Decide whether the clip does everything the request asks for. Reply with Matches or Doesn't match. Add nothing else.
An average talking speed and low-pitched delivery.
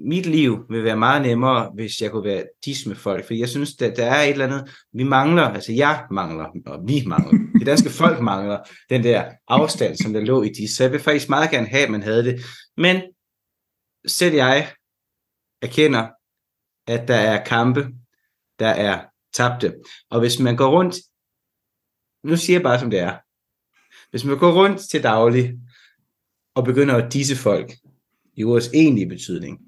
Matches